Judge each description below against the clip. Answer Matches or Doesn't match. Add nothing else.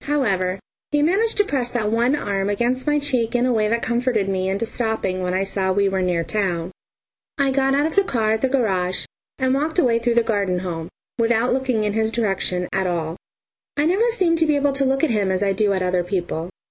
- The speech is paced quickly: Matches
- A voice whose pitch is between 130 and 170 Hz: Doesn't match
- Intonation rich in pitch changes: Matches